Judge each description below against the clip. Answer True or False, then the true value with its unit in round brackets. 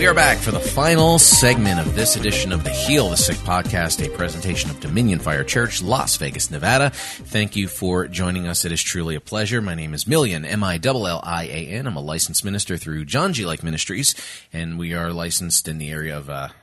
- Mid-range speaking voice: False (85 Hz)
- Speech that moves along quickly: True (210 wpm)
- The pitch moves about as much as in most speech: True (4.3 semitones)